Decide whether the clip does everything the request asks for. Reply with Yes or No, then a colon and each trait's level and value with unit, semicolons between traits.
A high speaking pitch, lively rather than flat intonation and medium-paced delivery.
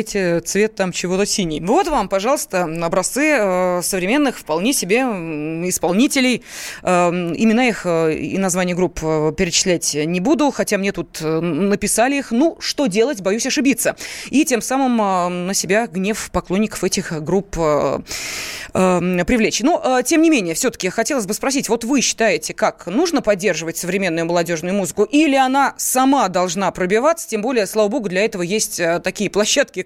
Yes: high, 205 Hz; wide, 5.9 semitones; average, 145 wpm